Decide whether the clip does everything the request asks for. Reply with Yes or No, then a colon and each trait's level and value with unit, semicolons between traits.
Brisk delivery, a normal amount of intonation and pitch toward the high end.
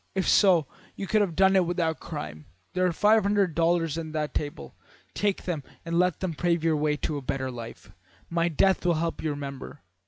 No: fast, 215 wpm; average, 3.6 semitones; medium, 165 Hz